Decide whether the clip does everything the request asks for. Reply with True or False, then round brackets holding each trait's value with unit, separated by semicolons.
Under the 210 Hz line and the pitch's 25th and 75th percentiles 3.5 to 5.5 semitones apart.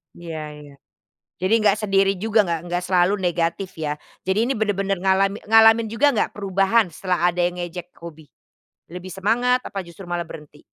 False (190 Hz; 3.0 semitones)